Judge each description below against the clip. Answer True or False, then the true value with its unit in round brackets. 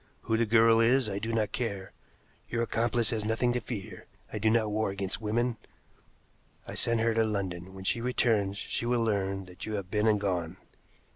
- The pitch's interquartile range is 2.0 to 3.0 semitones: True (2.7 semitones)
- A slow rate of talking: False (200 wpm)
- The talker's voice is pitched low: True (110 Hz)